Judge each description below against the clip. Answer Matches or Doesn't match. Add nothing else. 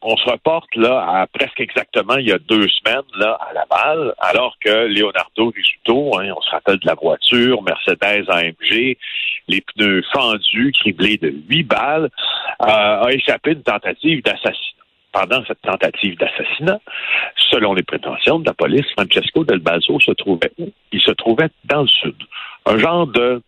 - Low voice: Matches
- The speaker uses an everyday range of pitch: Doesn't match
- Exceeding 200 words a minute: Doesn't match